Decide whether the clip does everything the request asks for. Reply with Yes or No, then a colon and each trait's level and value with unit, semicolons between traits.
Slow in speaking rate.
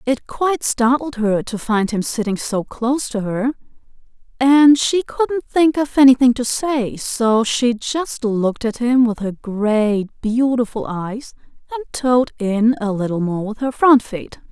No: average, 170 wpm